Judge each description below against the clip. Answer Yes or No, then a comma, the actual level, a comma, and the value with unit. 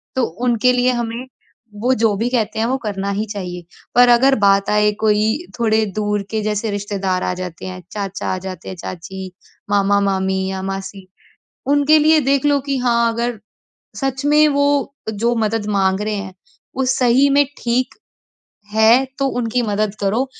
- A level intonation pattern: No, average, 4.1 semitones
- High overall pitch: Yes, high, 220 Hz